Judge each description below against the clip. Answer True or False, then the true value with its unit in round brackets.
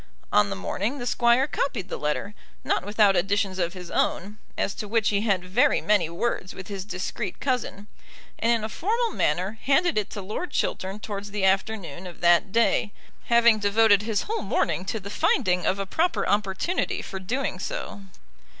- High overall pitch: True (205 Hz)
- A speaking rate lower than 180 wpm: False (185 wpm)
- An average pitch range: True (3.5 semitones)